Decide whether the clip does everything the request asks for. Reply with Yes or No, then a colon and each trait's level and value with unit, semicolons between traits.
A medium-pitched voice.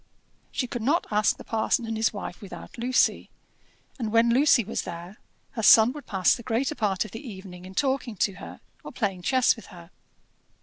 No: high, 225 Hz